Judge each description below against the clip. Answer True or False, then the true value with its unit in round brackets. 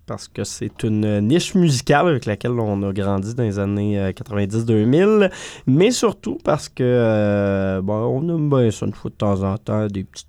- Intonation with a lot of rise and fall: True (6.2 semitones)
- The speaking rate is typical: True (195 wpm)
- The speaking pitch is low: True (110 Hz)